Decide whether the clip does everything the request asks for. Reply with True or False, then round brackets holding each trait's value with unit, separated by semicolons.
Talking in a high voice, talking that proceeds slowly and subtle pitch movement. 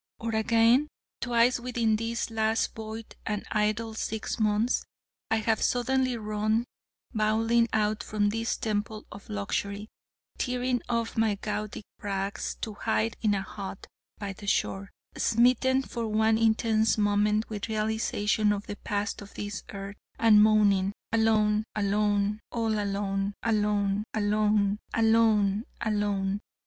True (215 Hz; 130 wpm; 1.6 semitones)